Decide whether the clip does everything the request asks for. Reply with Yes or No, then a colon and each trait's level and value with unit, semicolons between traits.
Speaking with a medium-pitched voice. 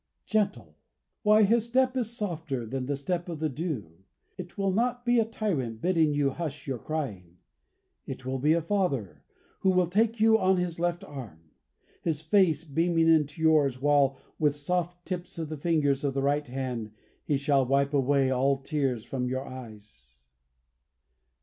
Yes: medium, 150 Hz